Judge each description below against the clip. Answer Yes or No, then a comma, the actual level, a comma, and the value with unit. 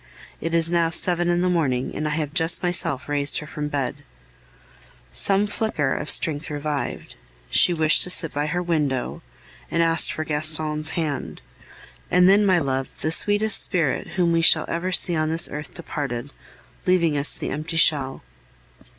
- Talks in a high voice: No, medium, 160 Hz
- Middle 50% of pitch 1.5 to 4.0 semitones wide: Yes, average, 2.9 semitones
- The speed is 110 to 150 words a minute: No, average, 170 wpm